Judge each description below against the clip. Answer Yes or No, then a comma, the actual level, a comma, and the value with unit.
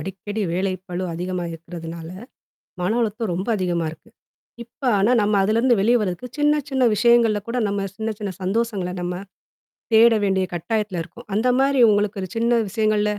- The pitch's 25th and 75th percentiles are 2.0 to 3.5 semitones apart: No, average, 4.0 semitones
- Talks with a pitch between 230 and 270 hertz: No, high, 205 Hz